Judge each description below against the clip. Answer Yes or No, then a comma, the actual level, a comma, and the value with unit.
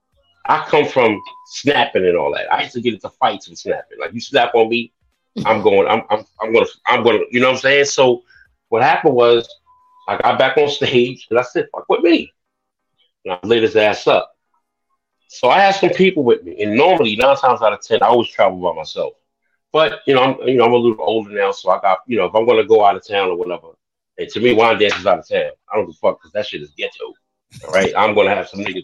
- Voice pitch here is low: No, high, 190 Hz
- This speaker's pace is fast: Yes, fast, 255 wpm